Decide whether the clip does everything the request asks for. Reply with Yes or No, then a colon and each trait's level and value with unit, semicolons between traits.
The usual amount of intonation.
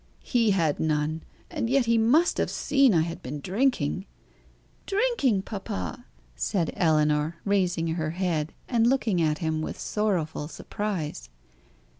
No: wide, 6.5 semitones